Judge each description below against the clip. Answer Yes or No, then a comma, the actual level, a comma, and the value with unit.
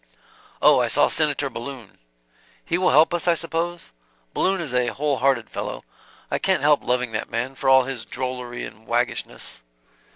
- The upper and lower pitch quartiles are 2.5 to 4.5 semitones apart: Yes, average, 3.6 semitones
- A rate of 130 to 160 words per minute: No, average, 170 wpm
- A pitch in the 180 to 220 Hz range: No, low, 135 Hz